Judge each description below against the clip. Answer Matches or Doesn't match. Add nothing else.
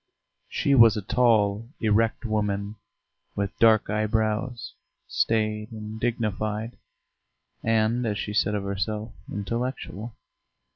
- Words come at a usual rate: Doesn't match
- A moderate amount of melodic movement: Doesn't match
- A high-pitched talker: Doesn't match